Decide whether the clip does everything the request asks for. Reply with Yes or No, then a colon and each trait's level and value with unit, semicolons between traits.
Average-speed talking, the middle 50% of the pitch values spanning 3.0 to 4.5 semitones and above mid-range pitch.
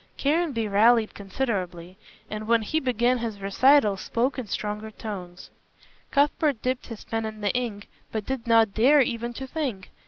Yes: average, 160 wpm; average, 3.6 semitones; high, 230 Hz